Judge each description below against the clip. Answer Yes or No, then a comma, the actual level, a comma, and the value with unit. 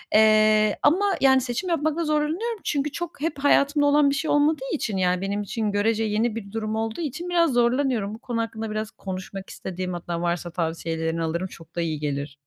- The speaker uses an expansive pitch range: Yes, wide, 7.5 semitones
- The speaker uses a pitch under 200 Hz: No, high, 225 Hz